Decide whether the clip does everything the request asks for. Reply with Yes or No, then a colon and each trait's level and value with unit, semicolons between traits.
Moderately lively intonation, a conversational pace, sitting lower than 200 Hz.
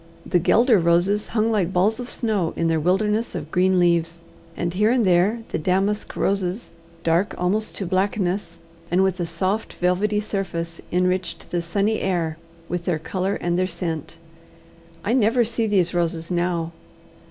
Yes: average, 3.3 semitones; average, 165 wpm; medium, 185 Hz